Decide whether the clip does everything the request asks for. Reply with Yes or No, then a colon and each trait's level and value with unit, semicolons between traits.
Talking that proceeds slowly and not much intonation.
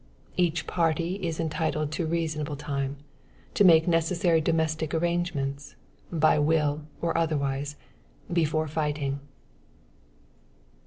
Yes: slow, 105 wpm; narrow, 2.1 semitones